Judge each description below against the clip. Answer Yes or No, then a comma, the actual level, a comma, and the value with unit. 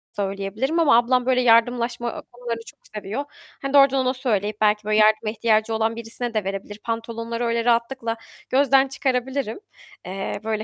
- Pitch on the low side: No, high, 230 Hz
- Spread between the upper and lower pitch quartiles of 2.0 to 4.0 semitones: Yes, average, 2.7 semitones